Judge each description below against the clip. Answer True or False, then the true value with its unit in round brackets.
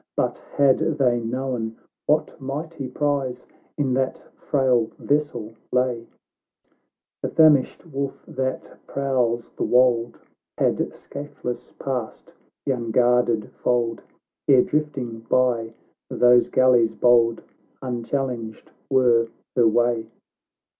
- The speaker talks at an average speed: False (100 wpm)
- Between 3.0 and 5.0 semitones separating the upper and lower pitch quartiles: False (2.5 semitones)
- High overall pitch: False (125 Hz)